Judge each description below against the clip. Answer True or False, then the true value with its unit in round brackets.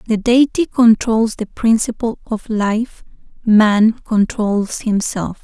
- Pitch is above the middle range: True (220 Hz)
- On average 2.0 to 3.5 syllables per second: True (3.4 syllables/s)